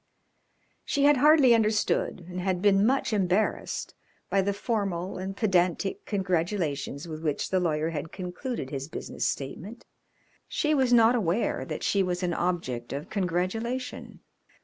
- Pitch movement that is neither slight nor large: Yes, average, 4.5 semitones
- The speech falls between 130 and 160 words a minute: Yes, average, 145 wpm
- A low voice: No, high, 190 Hz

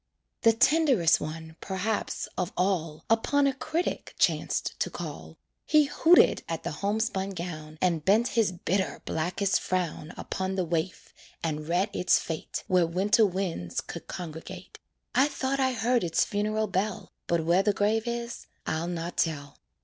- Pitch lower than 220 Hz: Yes, high, 190 Hz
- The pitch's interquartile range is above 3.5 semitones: Yes, average, 5.1 semitones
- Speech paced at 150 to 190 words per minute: Yes, average, 155 wpm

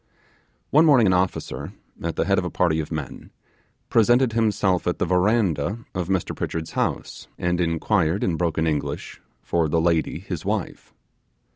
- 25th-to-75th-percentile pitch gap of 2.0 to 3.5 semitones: No, average, 4.2 semitones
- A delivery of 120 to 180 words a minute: Yes, average, 160 wpm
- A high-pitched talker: No, very low, 90 Hz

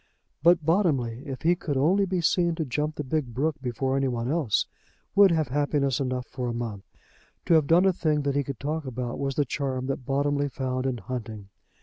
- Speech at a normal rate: No, fast, 215 wpm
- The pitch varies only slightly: No, average, 3.7 semitones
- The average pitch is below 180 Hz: Yes, medium, 140 Hz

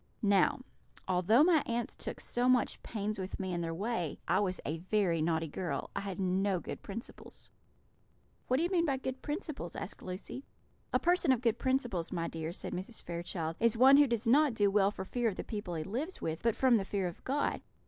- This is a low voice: No, high, 205 Hz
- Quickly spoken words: Yes, fast, 215 wpm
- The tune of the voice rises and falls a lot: Yes, wide, 6.2 semitones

